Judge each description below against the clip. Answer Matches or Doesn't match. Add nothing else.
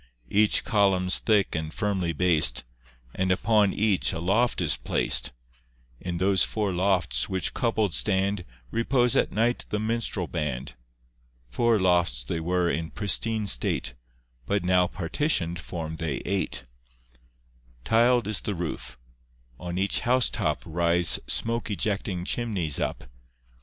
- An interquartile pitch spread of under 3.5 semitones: Doesn't match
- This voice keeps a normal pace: Doesn't match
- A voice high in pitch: Doesn't match